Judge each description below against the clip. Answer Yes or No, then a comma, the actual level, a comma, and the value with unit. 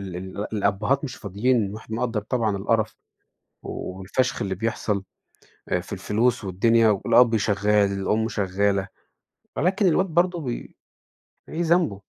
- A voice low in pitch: Yes, low, 110 Hz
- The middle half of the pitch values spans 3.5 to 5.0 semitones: Yes, average, 4.1 semitones